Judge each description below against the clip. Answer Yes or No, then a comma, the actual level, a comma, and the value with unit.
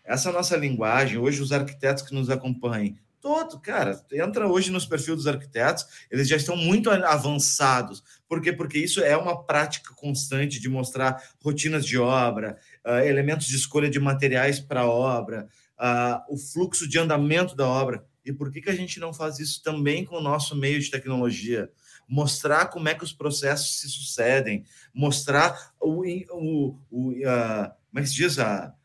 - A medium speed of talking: Yes, average, 170 wpm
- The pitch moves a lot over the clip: No, average, 3.1 semitones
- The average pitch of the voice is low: No, medium, 145 Hz